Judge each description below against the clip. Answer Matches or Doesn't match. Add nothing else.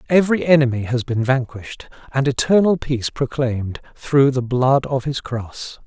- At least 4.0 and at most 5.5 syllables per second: Matches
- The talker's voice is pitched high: Doesn't match